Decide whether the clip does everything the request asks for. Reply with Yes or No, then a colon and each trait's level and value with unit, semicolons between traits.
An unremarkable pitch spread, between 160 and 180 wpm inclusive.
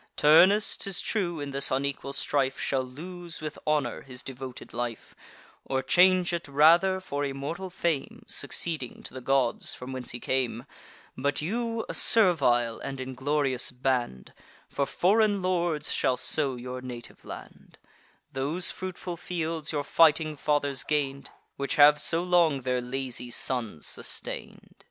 No: average, 4.7 semitones; average, 140 wpm